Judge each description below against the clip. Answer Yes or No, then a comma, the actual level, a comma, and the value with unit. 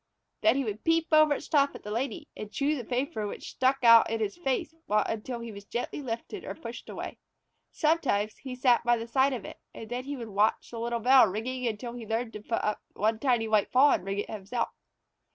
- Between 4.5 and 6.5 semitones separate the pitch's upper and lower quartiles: No, average, 3.7 semitones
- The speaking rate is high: Yes, fast, 230 wpm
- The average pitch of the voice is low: No, high, 235 Hz